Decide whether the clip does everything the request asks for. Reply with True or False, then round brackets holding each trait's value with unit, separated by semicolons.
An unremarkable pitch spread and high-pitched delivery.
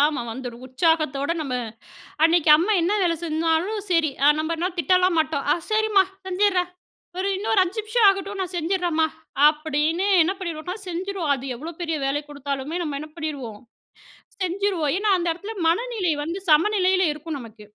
True (3.9 semitones; 335 Hz)